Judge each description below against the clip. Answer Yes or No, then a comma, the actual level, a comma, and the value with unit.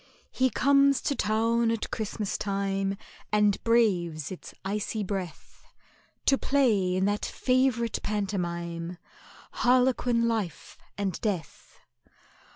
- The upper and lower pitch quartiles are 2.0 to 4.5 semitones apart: Yes, average, 3.6 semitones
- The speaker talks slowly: Yes, slow, 105 wpm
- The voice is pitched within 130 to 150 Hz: No, high, 210 Hz